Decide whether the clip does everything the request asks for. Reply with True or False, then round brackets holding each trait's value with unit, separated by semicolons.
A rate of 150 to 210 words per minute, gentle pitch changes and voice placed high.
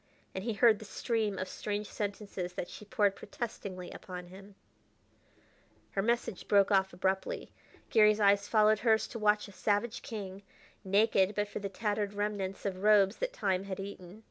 True (170 wpm; 1.7 semitones; 205 Hz)